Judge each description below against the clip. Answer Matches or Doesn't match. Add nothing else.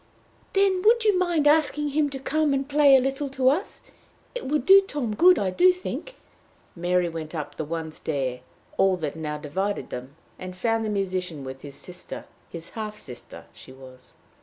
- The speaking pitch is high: Matches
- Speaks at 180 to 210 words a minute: Matches